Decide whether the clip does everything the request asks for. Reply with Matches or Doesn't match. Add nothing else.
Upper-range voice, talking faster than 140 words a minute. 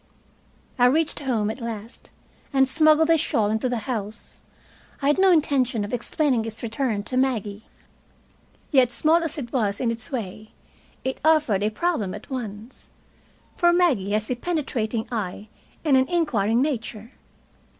Matches